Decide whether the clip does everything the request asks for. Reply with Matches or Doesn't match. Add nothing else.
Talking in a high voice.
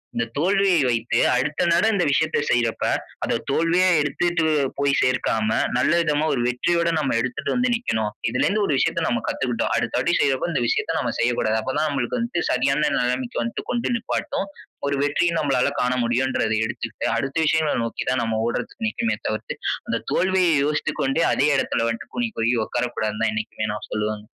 Doesn't match